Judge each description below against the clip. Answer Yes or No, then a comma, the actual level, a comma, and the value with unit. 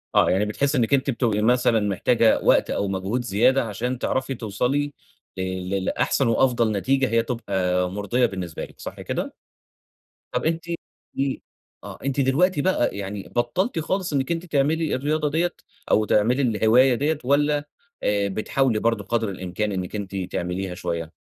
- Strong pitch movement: Yes, wide, 5.7 semitones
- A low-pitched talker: Yes, low, 120 Hz